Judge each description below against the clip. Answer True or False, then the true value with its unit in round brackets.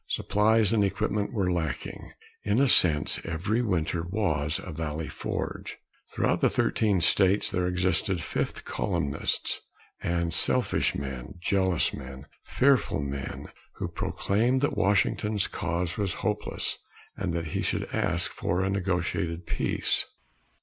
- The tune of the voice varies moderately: True (4.0 semitones)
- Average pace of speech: False (130 wpm)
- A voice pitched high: False (90 Hz)